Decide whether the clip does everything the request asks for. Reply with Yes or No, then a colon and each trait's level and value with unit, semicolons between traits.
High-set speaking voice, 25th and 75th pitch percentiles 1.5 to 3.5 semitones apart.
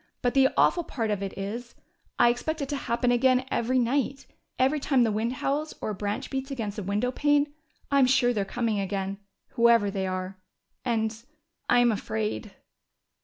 No: high, 235 Hz; average, 4.5 semitones